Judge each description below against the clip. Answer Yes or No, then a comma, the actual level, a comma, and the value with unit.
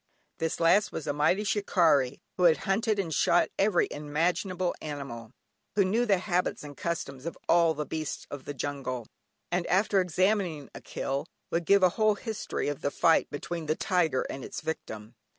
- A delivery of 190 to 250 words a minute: No, average, 180 wpm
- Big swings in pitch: No, average, 4.5 semitones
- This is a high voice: No, medium, 165 Hz